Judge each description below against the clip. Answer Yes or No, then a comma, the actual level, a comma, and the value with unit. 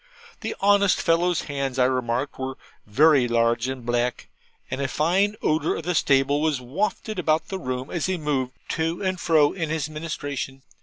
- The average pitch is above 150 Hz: No, medium, 145 Hz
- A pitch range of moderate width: Yes, average, 4.3 semitones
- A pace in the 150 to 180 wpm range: Yes, average, 175 wpm